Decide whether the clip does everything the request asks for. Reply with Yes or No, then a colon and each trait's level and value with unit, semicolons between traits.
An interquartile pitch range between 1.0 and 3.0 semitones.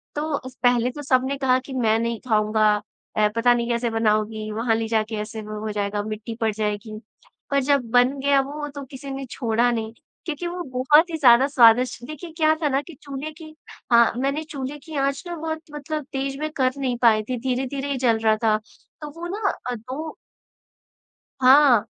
No: average, 4.2 semitones